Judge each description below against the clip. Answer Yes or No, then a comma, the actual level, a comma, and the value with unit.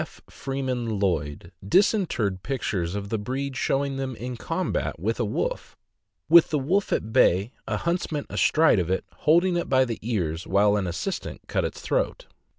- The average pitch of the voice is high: No, low, 125 Hz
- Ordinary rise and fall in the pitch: No, wide, 6.6 semitones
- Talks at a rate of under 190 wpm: Yes, average, 165 wpm